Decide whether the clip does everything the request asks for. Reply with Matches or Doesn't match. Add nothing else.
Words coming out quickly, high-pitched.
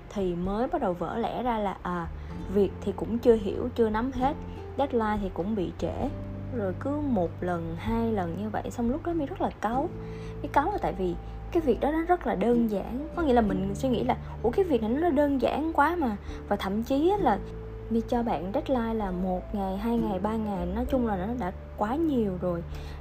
Doesn't match